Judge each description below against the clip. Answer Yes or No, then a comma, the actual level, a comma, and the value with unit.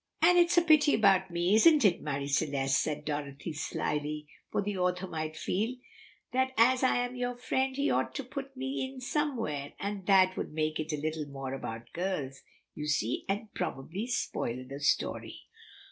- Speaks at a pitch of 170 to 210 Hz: Yes, medium, 185 Hz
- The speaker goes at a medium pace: Yes, average, 175 wpm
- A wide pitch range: Yes, wide, 8.9 semitones